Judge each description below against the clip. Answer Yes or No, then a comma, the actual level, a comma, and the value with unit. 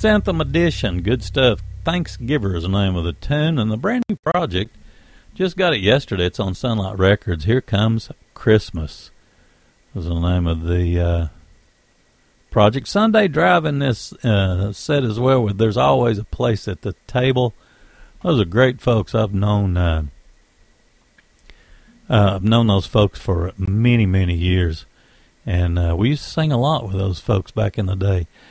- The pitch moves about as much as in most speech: No, wide, 5.9 semitones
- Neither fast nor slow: Yes, average, 170 wpm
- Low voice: Yes, low, 105 Hz